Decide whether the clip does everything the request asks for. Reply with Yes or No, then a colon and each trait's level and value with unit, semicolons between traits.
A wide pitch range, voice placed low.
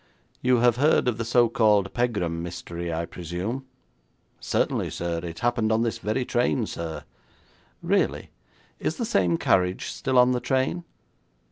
Yes: wide, 6.0 semitones; low, 110 Hz